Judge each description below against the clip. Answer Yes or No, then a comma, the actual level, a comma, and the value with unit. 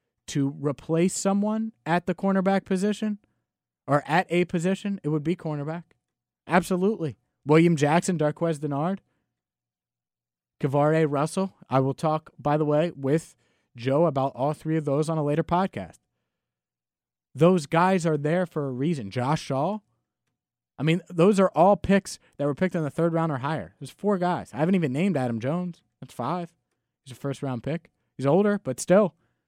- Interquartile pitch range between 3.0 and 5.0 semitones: Yes, average, 4.7 semitones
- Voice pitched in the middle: Yes, medium, 155 Hz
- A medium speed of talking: Yes, average, 170 wpm